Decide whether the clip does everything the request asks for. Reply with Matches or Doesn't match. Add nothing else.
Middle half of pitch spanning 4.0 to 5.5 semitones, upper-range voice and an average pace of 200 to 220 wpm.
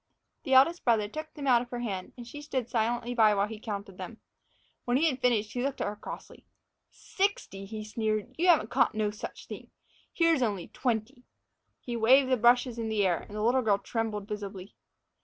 Doesn't match